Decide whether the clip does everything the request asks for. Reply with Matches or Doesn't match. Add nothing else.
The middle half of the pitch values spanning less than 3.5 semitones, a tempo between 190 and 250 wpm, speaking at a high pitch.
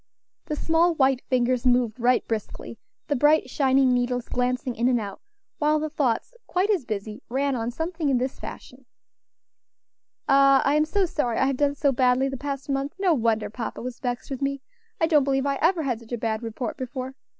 Matches